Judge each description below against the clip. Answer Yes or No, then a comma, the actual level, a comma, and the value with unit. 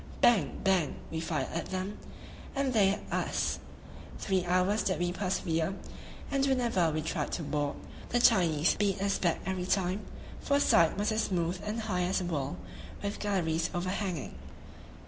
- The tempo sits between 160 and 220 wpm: Yes, average, 170 wpm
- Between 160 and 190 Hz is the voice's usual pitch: Yes, medium, 185 Hz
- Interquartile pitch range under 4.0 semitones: Yes, average, 3.4 semitones